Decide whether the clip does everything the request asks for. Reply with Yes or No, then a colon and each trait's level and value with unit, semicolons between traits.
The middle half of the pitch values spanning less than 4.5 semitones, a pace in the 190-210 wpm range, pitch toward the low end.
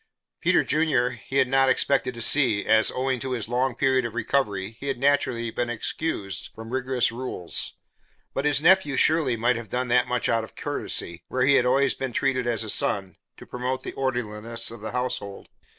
Yes: average, 2.7 semitones; average, 200 wpm; low, 125 Hz